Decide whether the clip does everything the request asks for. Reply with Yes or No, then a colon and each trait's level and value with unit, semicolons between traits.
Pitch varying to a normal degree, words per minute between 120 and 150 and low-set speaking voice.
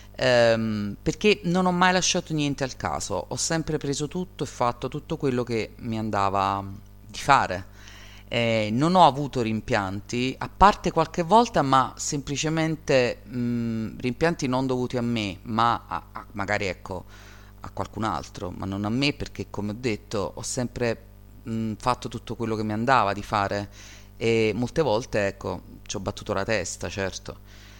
No: average, 4.8 semitones; average, 160 wpm; low, 110 Hz